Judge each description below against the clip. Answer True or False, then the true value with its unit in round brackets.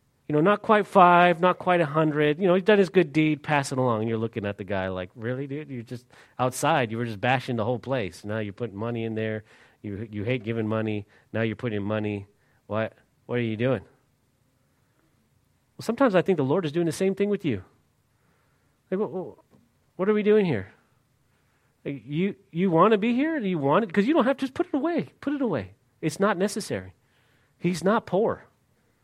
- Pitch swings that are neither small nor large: False (8.4 semitones)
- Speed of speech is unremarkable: False (215 wpm)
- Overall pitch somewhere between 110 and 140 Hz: True (135 Hz)